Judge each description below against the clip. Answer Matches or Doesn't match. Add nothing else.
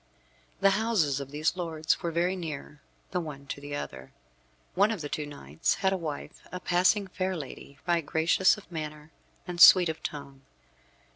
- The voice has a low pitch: Doesn't match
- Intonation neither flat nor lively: Matches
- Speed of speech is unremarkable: Matches